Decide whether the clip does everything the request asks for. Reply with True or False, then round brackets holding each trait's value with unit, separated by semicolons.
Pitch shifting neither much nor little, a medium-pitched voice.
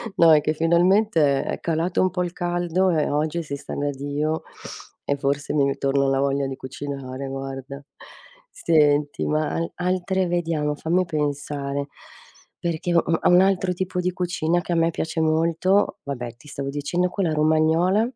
True (3.7 semitones; 155 Hz)